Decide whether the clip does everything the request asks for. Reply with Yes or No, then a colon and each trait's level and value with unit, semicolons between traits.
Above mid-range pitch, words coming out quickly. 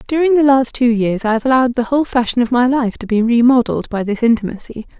Yes: high, 240 Hz; fast, 240 wpm